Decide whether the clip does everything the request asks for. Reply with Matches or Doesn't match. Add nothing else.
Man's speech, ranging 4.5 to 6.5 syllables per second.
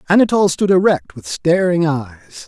Matches